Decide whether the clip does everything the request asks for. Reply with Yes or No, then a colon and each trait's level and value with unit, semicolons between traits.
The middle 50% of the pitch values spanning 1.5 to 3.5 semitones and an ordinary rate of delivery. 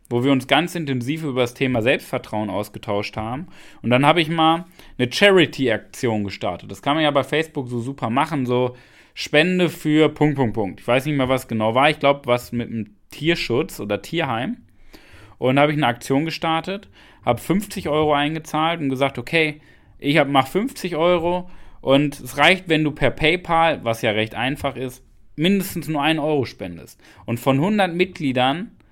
No: average, 4.4 semitones; average, 180 wpm